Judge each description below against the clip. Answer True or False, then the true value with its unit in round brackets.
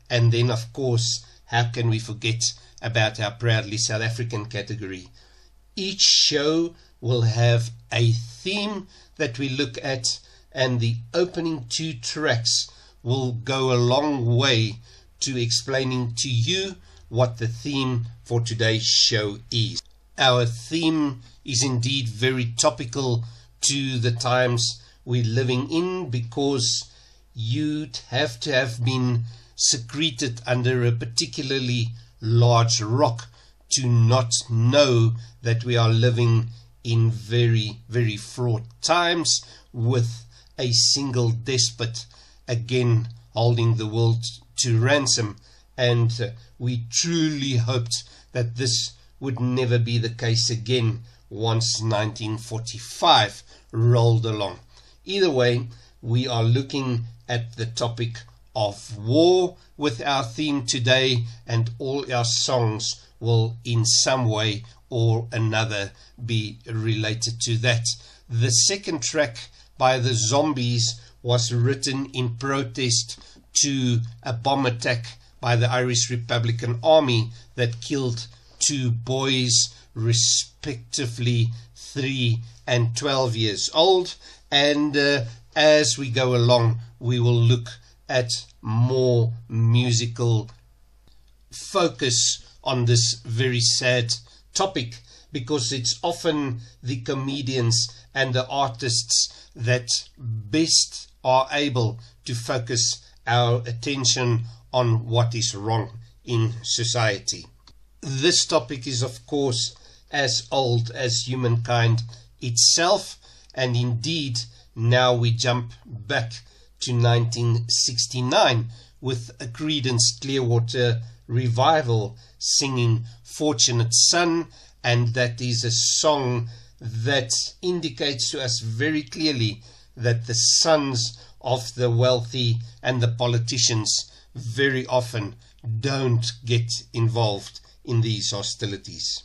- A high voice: False (120 Hz)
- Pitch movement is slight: True (1.9 semitones)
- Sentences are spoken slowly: True (110 wpm)